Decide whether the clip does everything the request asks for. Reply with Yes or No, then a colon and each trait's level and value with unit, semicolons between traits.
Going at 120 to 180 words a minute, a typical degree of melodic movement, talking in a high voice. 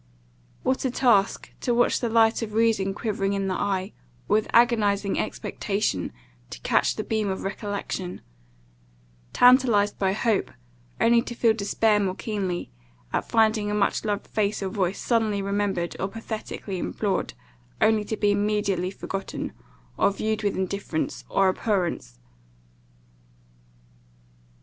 No: slow, 135 wpm; narrow, 2.2 semitones; high, 205 Hz